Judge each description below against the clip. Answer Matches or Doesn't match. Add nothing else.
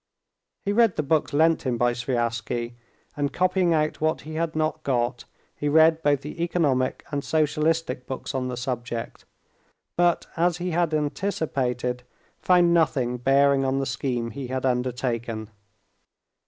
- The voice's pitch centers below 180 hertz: Matches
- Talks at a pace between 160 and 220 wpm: Doesn't match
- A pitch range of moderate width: Matches